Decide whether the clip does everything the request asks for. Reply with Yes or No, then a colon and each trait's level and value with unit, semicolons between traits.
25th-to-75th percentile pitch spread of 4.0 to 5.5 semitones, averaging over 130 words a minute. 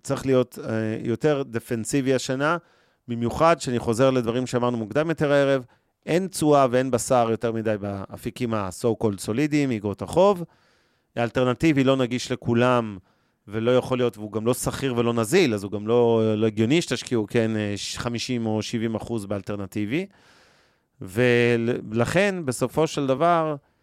No: average, 3.3 semitones; average, 140 wpm